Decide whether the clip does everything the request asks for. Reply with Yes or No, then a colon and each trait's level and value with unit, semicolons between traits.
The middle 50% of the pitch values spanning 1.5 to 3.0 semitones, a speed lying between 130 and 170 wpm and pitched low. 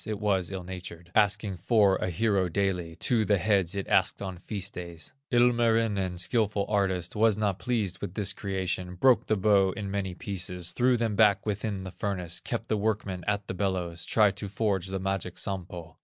No: narrow, 2.6 semitones; average, 185 wpm; low, 100 Hz